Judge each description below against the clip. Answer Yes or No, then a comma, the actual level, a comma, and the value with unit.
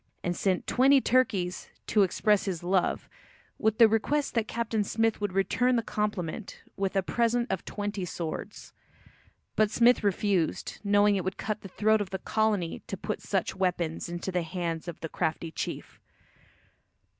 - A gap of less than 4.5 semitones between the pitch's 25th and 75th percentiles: Yes, average, 3.4 semitones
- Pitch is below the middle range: No, high, 200 Hz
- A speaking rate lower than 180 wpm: Yes, average, 165 wpm